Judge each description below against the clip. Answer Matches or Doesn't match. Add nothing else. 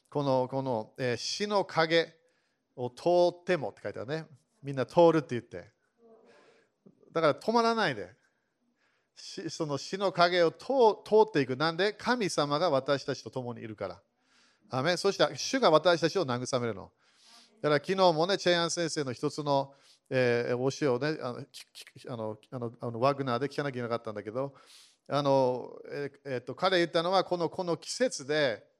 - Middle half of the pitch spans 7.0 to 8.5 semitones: Doesn't match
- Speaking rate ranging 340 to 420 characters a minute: Doesn't match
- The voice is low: Doesn't match